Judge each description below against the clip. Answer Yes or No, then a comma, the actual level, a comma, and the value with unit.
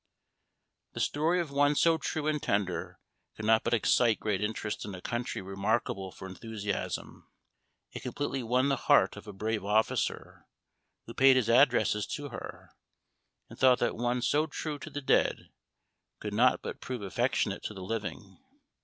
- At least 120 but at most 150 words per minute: No, average, 165 wpm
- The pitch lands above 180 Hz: No, low, 120 Hz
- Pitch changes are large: No, average, 4.8 semitones